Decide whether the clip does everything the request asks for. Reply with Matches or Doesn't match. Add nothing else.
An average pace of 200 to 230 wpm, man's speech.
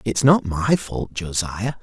Doesn't match